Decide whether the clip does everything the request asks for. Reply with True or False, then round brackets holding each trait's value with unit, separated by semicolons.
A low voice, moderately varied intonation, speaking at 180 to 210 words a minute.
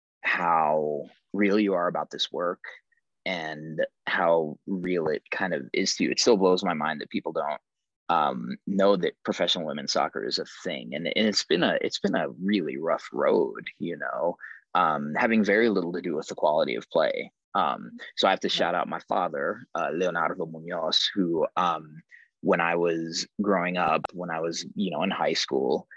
True (85 Hz; 3.7 semitones; 195 wpm)